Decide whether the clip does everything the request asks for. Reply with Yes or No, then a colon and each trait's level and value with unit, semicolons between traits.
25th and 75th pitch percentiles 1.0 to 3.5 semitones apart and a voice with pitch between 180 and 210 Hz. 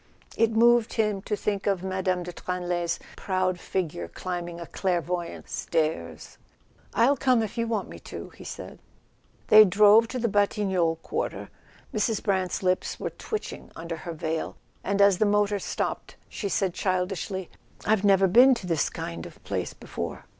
Yes: average, 3.2 semitones; high, 190 Hz